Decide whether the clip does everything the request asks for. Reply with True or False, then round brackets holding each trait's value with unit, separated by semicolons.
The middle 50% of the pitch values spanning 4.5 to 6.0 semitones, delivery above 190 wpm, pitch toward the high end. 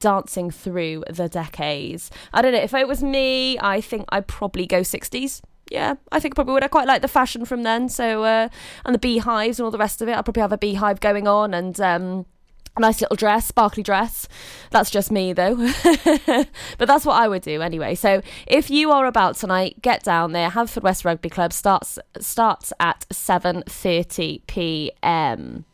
True (5.1 semitones; 200 wpm; 215 Hz)